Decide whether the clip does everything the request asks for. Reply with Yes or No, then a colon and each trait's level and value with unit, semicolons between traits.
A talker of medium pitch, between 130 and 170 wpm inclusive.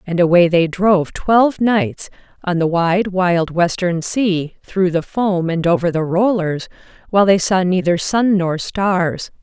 Yes: medium, 180 Hz; average, 165 wpm